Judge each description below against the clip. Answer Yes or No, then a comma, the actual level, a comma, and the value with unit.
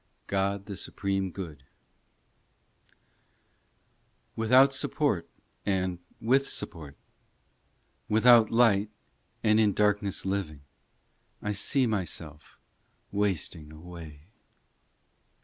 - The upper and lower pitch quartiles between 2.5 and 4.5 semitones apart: Yes, average, 4.0 semitones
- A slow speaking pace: Yes, slow, 80 wpm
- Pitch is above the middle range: No, low, 100 Hz